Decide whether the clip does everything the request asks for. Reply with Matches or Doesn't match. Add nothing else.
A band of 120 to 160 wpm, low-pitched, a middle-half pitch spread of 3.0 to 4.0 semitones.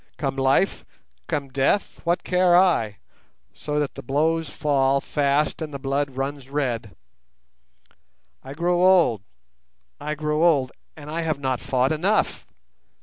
Doesn't match